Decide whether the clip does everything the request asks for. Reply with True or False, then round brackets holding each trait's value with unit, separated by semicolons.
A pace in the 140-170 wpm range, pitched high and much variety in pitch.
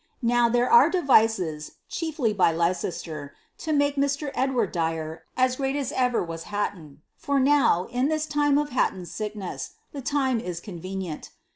True (160 wpm; 235 Hz; 8.3 semitones)